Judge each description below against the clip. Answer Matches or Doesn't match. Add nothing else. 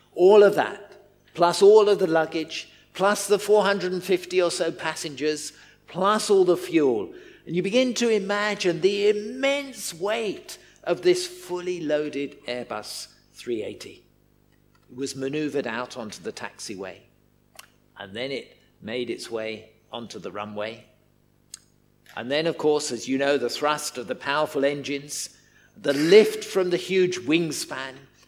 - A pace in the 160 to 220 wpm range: Doesn't match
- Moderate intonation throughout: Doesn't match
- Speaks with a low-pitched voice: Doesn't match